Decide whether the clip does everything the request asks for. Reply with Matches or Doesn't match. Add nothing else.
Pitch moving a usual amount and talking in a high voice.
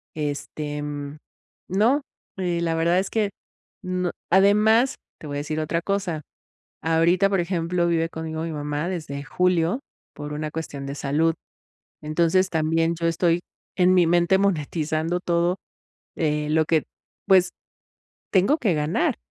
Doesn't match